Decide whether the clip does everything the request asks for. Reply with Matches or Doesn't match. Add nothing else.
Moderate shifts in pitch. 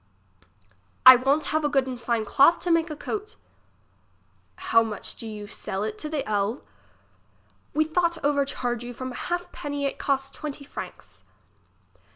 Matches